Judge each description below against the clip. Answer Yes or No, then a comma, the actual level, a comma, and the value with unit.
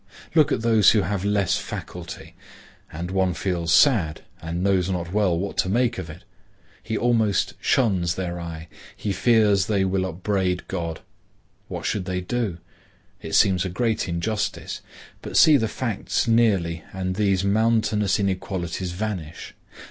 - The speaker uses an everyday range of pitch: Yes, average, 3.4 semitones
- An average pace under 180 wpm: Yes, average, 150 wpm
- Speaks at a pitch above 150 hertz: No, very low, 95 Hz